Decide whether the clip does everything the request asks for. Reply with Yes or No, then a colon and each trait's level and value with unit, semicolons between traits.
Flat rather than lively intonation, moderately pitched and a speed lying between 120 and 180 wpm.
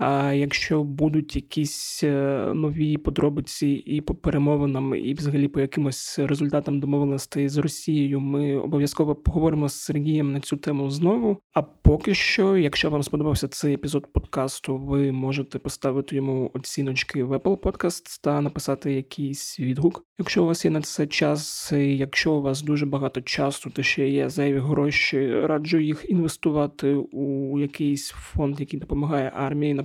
Yes: narrow, 1.7 semitones; medium, 145 Hz; average, 150 wpm